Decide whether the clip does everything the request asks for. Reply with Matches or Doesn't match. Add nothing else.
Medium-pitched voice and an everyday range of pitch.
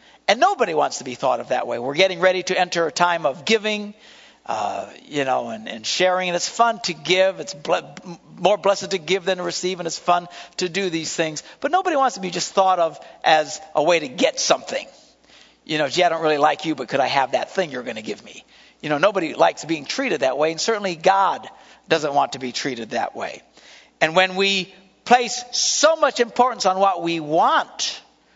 Matches